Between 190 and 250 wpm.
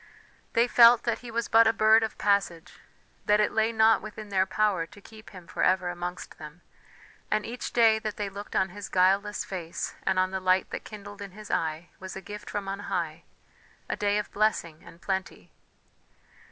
Yes: average, 200 wpm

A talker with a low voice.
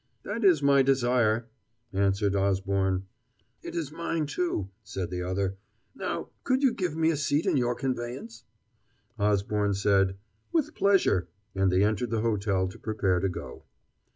Yes: low, 110 Hz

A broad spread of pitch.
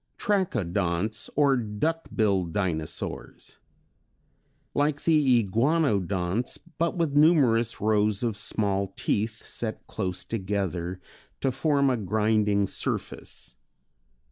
Yes: wide, 5.9 semitones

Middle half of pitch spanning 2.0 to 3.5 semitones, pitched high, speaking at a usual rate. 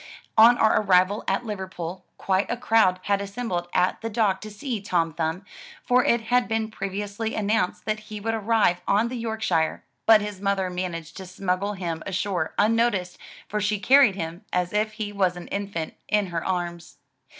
Yes: average, 3.2 semitones; high, 200 Hz; average, 180 wpm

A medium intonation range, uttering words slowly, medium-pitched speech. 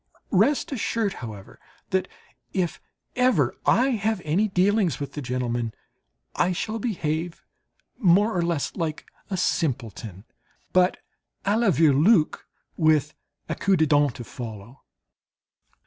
No: wide, 6.7 semitones; slow, 125 wpm; medium, 170 Hz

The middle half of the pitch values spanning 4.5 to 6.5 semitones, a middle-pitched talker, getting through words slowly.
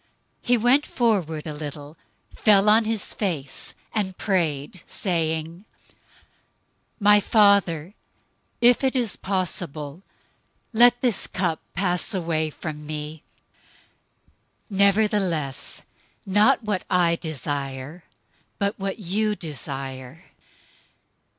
Yes: average, 5.2 semitones; medium, 180 Hz; slow, 100 wpm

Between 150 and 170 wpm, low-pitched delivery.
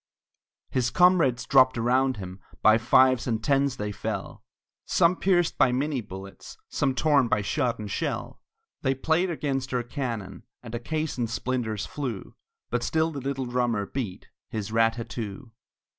Yes: average, 160 wpm; low, 125 Hz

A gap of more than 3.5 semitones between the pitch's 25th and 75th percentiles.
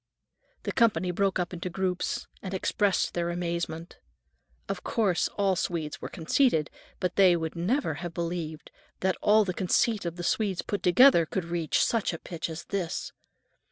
No: average, 2.7 semitones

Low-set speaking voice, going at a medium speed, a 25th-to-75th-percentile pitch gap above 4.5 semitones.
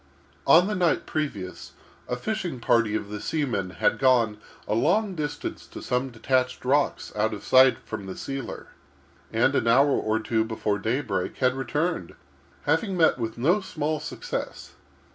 Yes: low, 130 Hz; average, 160 wpm; wide, 5.6 semitones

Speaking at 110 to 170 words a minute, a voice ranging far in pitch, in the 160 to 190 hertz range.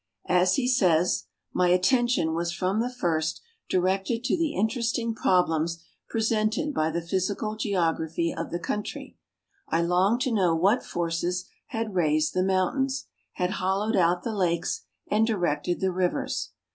No: average, 145 wpm; average, 4.4 semitones; medium, 185 Hz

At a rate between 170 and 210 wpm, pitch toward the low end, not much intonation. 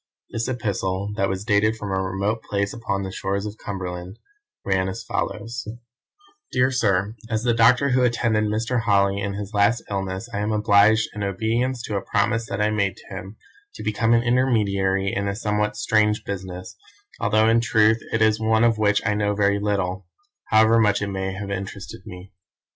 Yes: average, 185 wpm; low, 105 Hz; narrow, 2.2 semitones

